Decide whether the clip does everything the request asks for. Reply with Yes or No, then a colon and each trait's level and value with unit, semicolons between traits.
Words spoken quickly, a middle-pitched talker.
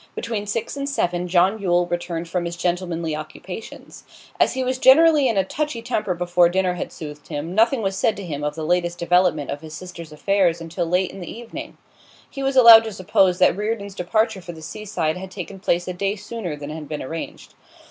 Yes: fast, 210 wpm; medium, 180 Hz